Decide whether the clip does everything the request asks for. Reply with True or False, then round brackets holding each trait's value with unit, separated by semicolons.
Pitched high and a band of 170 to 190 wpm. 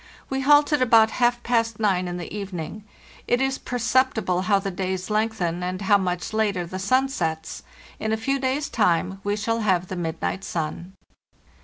True (205 Hz; 175 wpm)